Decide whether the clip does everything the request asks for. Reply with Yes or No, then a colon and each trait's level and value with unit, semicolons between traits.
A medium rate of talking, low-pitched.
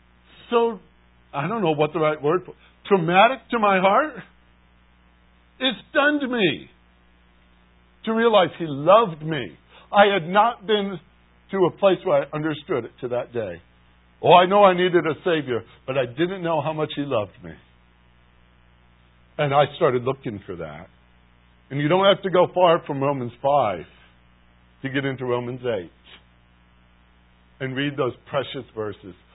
Yes: average, 155 wpm; low, 130 Hz